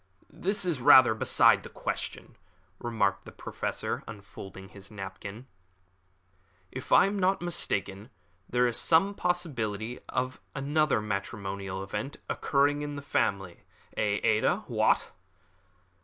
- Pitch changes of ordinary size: No, wide, 6.8 semitones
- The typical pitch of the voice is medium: No, low, 120 Hz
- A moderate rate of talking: No, slow, 125 wpm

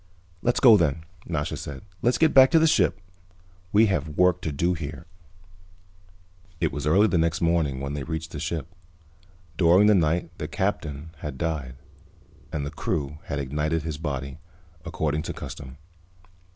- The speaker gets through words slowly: No, average, 165 wpm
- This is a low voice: Yes, very low, 80 Hz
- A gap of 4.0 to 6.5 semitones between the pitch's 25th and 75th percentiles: No, average, 3.3 semitones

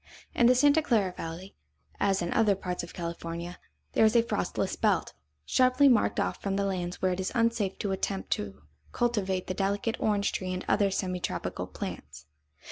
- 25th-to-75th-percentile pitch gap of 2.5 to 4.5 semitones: Yes, average, 3.7 semitones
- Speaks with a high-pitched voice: Yes, high, 195 Hz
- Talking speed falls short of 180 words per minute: No, average, 185 wpm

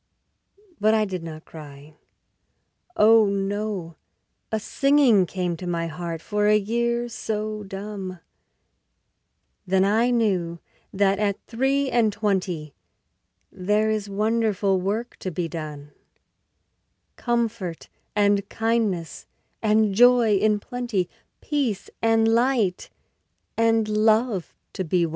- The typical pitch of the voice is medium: No, high, 210 Hz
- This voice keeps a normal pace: No, slow, 115 wpm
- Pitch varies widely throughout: No, average, 3.5 semitones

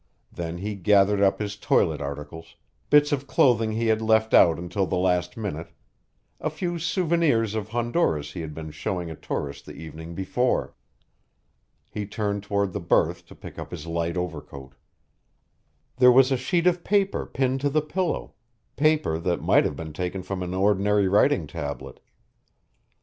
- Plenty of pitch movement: Yes, wide, 6.9 semitones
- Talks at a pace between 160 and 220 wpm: Yes, average, 165 wpm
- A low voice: Yes, low, 100 Hz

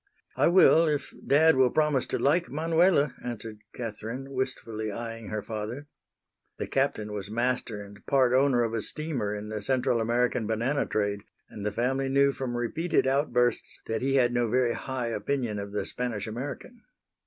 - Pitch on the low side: Yes, low, 125 Hz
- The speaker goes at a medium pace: Yes, average, 170 wpm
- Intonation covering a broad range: No, average, 3.9 semitones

